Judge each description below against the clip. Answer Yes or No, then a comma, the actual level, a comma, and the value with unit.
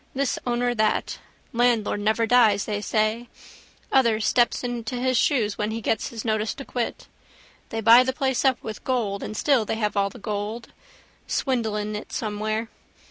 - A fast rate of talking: No, average, 175 wpm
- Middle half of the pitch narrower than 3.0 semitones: Yes, narrow, 2.4 semitones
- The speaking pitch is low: No, high, 225 Hz